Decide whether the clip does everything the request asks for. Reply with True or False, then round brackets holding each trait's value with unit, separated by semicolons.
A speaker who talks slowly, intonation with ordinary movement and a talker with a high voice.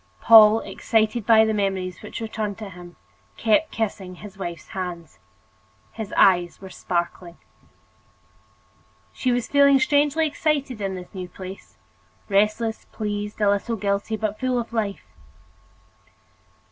True (130 wpm; 3.2 semitones; 210 Hz)